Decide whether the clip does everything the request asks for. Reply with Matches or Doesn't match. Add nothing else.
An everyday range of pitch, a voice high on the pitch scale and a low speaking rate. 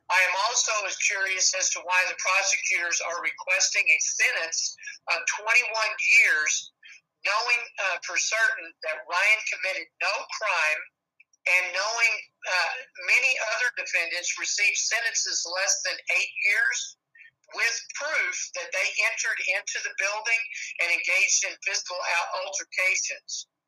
Doesn't match